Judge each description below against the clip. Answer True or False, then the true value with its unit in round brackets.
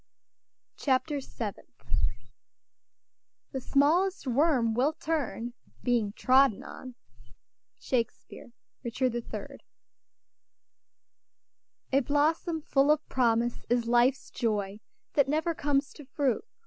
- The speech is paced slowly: True (95 wpm)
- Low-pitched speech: False (265 Hz)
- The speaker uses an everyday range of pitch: True (3.7 semitones)